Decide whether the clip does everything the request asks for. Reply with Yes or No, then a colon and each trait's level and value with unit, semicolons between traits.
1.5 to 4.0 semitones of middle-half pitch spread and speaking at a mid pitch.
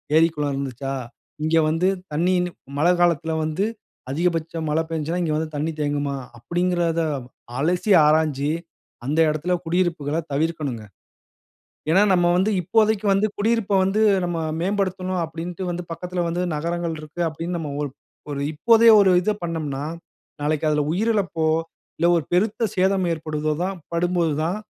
Yes: average, 2.8 semitones; medium, 165 Hz